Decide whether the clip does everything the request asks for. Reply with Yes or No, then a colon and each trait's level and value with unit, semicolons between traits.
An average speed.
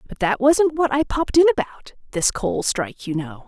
No: fast, 225 wpm